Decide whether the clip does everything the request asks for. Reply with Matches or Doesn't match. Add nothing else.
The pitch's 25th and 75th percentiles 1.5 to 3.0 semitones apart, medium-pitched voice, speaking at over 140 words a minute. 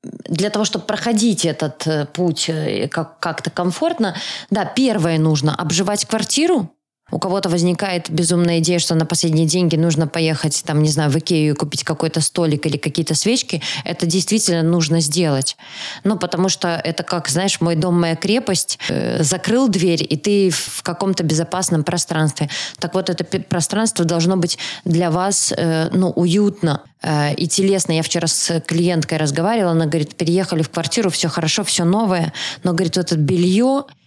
Matches